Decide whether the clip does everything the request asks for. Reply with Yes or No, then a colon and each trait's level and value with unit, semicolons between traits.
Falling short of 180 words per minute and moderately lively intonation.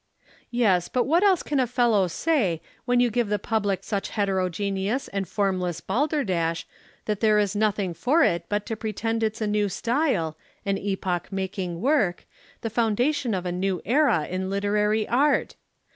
Yes: average, 165 wpm; average, 4.1 semitones